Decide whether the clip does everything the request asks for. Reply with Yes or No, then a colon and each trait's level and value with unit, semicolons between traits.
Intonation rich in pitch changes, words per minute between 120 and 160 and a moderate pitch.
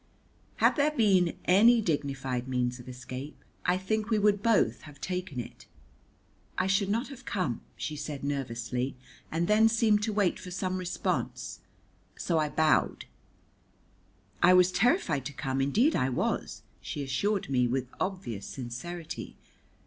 Yes: wide, 7.5 semitones; average, 150 wpm; medium, 175 Hz